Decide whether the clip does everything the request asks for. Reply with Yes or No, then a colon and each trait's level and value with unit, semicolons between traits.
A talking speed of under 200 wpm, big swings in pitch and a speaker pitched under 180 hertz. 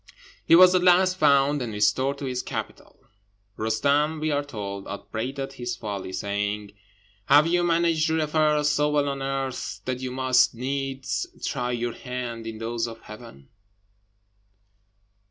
No: average, 150 wpm; average, 4.4 semitones; low, 135 Hz